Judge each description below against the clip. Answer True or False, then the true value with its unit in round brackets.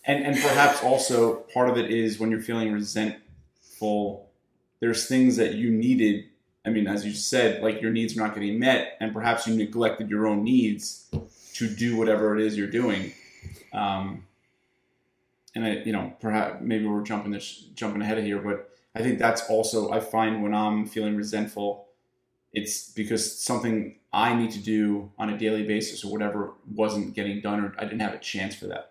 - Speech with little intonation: True (1.6 semitones)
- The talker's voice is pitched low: True (110 Hz)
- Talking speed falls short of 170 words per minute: False (190 wpm)